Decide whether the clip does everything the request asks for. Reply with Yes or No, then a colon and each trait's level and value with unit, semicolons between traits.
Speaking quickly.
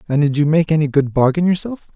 Yes: fast, 245 wpm